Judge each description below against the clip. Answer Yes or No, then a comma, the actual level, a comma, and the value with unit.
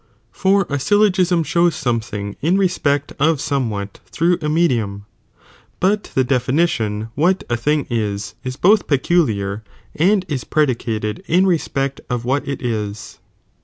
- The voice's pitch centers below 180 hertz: Yes, medium, 140 Hz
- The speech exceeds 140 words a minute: Yes, average, 155 wpm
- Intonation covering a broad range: Yes, wide, 7.5 semitones